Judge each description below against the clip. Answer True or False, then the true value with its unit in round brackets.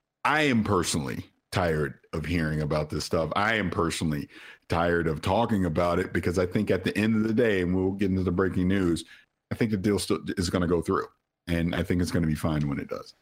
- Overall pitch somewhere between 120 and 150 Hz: False (90 Hz)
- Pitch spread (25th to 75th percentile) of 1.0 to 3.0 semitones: True (2.5 semitones)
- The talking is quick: True (245 wpm)